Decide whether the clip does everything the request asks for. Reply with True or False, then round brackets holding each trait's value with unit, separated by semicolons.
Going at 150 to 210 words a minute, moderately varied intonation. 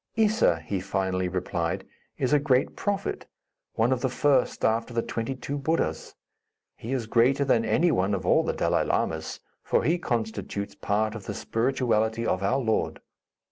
True (170 wpm; 4.8 semitones)